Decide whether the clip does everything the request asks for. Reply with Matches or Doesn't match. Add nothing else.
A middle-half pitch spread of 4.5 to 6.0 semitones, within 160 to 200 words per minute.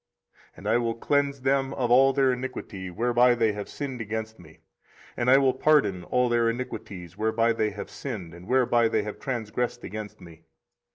Doesn't match